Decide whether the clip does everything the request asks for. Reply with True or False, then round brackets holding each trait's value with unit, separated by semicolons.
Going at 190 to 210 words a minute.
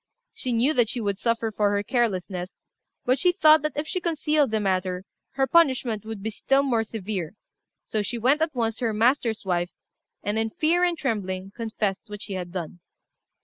True (195 wpm)